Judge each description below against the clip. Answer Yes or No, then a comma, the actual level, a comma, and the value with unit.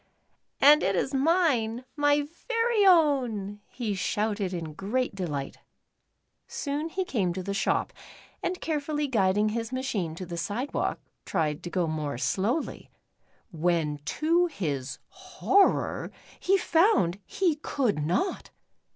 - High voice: Yes, high, 220 Hz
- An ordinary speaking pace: No, slow, 125 wpm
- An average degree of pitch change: No, wide, 9.0 semitones